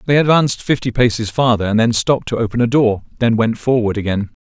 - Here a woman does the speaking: No, male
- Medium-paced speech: No, fast, 215 wpm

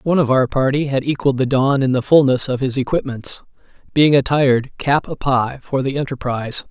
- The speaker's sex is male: Yes, male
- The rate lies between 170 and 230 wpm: Yes, average, 195 wpm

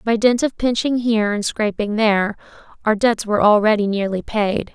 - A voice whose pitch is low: No, high, 215 Hz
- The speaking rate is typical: Yes, average, 175 wpm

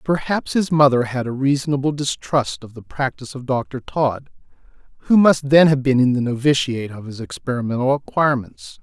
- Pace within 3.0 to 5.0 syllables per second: No, 5.4 syllables/s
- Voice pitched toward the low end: Yes, low, 130 Hz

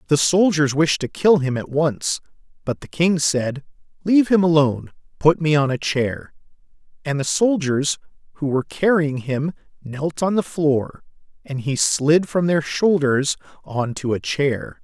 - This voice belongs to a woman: No, male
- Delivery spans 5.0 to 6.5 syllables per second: No, 4.3 syllables/s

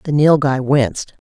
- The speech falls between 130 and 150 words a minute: Yes, average, 140 wpm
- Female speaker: Yes, female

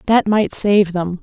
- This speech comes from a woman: Yes, female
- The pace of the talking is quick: No, average, 195 wpm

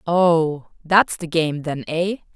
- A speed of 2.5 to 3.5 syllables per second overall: Yes, 3.2 syllables/s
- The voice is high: No, medium, 165 Hz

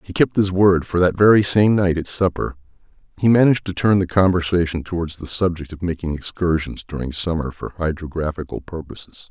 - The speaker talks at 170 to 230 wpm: Yes, average, 180 wpm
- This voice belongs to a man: Yes, male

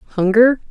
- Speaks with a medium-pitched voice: No, high, 220 Hz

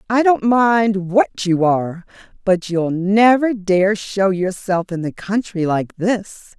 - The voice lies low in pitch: No, high, 195 Hz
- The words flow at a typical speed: Yes, average, 155 wpm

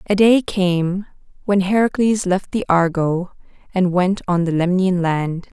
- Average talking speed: Yes, average, 150 wpm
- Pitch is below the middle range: No, medium, 185 Hz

